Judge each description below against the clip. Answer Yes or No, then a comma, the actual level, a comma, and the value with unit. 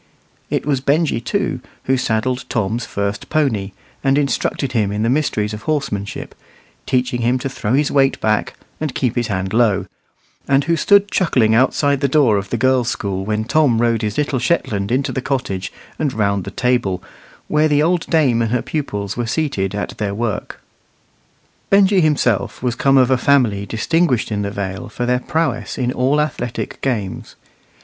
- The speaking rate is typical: Yes, average, 180 wpm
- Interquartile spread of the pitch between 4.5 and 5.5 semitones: Yes, average, 4.9 semitones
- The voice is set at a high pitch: No, low, 125 Hz